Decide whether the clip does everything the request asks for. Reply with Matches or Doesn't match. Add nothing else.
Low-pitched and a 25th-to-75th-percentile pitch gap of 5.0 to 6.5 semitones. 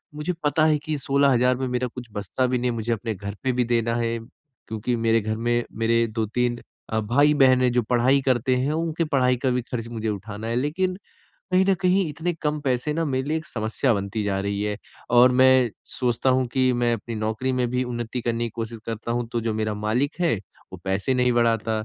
Doesn't match